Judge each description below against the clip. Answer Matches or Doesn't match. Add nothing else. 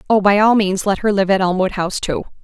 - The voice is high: Matches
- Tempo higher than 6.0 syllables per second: Matches